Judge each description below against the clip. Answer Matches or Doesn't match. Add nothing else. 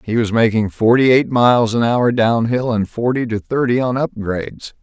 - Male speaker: Matches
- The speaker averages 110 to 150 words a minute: Doesn't match